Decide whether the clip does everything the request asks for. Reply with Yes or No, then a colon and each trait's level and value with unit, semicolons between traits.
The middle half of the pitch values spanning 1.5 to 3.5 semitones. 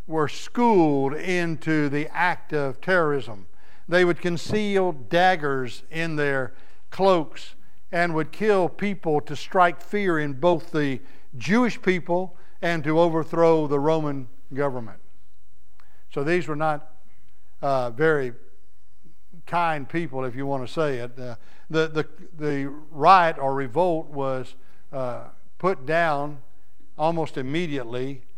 No: average, 4.4 semitones